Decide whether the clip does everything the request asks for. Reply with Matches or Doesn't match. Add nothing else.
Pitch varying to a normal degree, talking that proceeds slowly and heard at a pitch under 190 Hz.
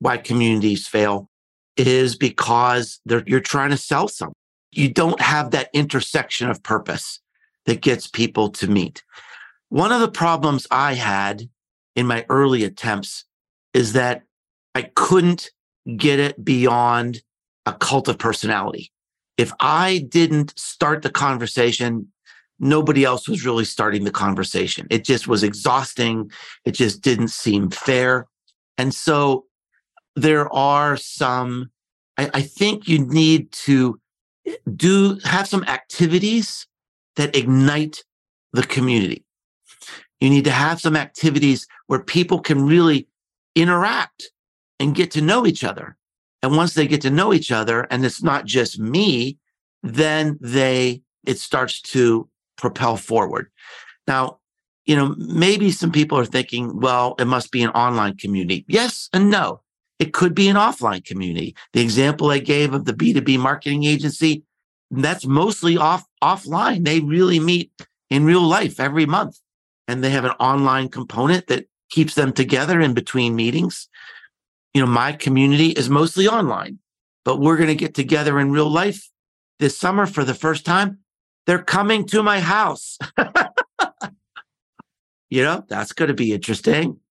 Doesn't match